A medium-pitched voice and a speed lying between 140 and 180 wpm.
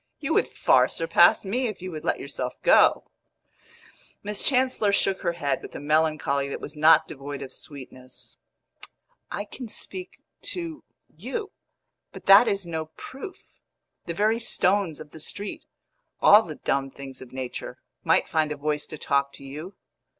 Yes: medium, 160 Hz; average, 165 wpm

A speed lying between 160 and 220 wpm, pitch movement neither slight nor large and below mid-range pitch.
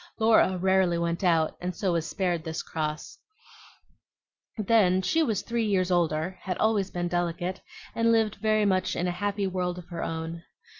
No: average, 165 wpm; average, 3.0 semitones; medium, 185 Hz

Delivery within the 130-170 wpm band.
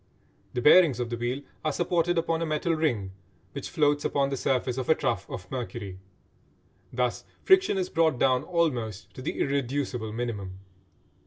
Yes: average, 165 wpm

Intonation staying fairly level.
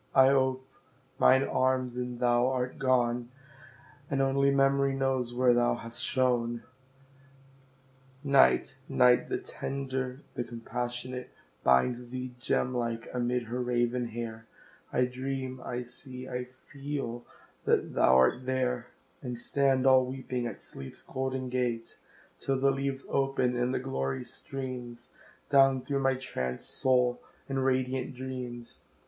Yes: narrow, 1.5 semitones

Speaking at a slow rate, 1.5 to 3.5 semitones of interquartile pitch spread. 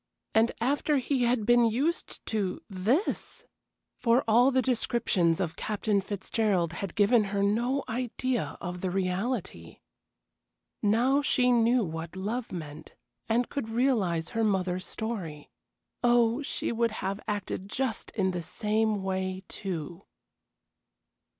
No: slow, 130 wpm; average, 4.4 semitones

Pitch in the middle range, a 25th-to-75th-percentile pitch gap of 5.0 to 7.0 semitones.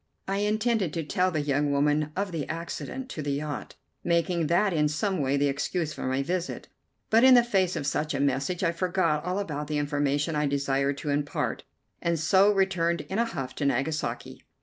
No: medium, 160 Hz; average, 4.4 semitones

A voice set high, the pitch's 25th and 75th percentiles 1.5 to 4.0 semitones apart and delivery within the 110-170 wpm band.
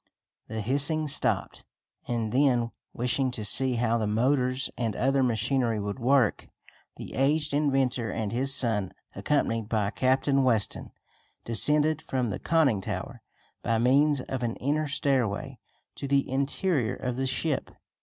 No: low, 130 Hz; average, 3.3 semitones; average, 145 wpm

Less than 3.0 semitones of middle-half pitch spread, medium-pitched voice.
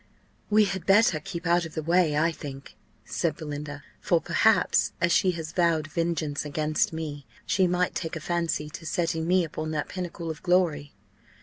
Yes: narrow, 2.5 semitones; medium, 165 Hz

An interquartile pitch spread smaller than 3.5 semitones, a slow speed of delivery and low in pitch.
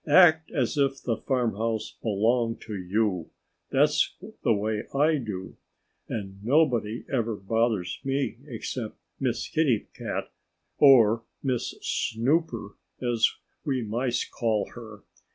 No: average, 3.8 semitones; slow, 115 wpm; low, 115 Hz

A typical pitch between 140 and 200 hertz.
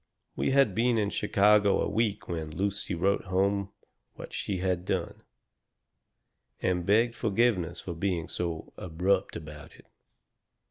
No: very low, 95 Hz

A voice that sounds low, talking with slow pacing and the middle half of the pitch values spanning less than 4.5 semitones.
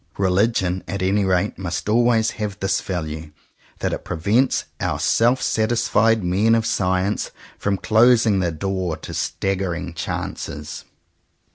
Yes: very low, 95 Hz; slow, 130 wpm; average, 3.6 semitones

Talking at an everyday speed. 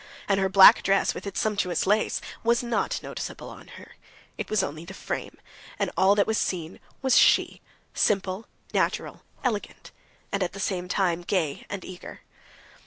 Yes: average, 165 wpm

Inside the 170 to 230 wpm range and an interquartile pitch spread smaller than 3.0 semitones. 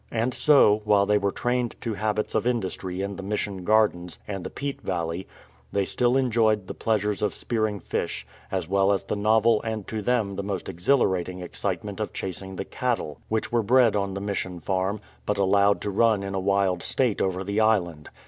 Yes: average, 195 wpm; narrow, 2.5 semitones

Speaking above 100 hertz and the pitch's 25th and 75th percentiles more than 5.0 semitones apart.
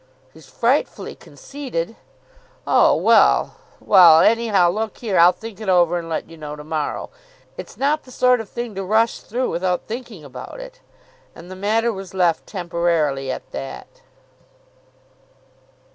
Yes: medium, 185 Hz; wide, 5.6 semitones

